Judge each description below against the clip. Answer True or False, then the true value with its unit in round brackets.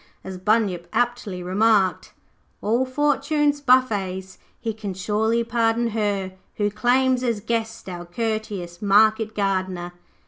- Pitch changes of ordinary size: True (3.6 semitones)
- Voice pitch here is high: True (215 Hz)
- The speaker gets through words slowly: True (115 wpm)